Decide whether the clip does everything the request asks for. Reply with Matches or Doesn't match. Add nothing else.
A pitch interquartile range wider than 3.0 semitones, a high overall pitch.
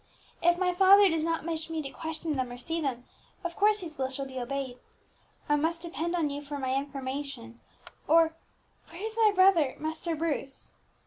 Matches